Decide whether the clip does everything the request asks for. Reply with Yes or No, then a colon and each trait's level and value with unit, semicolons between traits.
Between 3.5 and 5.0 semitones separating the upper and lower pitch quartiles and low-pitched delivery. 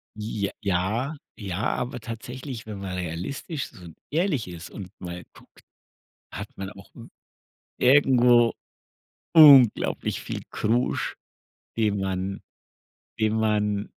Yes: average, 4.2 semitones; low, 110 Hz